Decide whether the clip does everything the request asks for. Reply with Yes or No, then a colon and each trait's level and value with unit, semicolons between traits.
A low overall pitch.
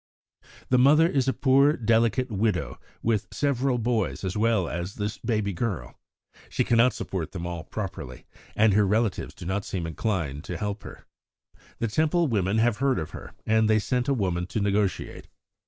Yes: low, 110 Hz